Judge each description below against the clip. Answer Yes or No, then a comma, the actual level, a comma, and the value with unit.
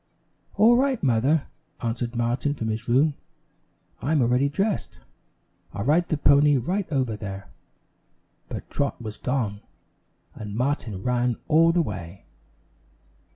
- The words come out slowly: Yes, slow, 125 wpm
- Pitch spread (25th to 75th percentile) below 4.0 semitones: No, average, 5.1 semitones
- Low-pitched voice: Yes, low, 125 Hz